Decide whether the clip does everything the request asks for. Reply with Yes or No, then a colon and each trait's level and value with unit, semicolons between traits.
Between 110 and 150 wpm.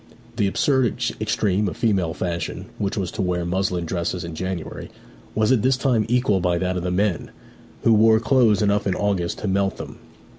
No: average, 190 wpm